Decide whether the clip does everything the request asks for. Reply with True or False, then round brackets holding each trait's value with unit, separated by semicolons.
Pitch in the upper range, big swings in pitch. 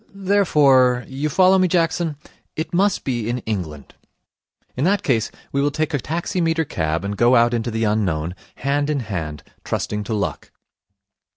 False (130 Hz; 7.1 semitones)